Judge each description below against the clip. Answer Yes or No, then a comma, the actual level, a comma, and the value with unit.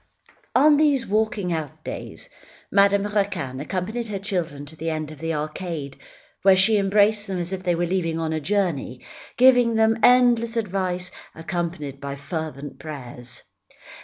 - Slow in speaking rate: No, average, 155 wpm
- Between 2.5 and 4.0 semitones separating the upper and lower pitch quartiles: No, average, 5.1 semitones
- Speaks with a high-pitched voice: No, medium, 180 Hz